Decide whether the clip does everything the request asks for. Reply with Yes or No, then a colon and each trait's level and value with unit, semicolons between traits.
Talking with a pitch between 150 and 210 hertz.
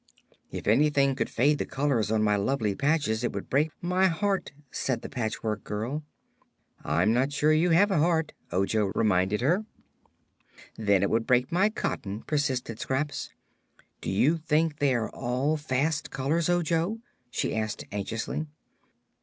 No: low, 135 Hz